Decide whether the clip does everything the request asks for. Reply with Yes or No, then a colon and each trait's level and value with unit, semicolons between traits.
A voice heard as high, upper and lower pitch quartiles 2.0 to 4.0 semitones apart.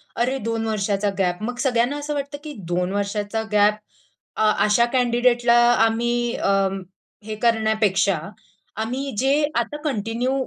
Yes: high, 230 Hz; average, 3.0 semitones